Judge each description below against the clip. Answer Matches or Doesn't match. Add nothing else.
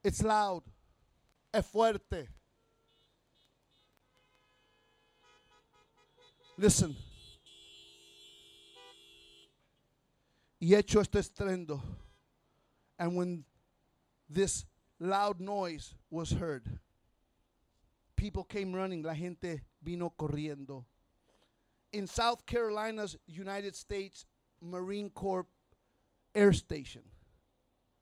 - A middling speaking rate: Doesn't match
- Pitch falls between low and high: Matches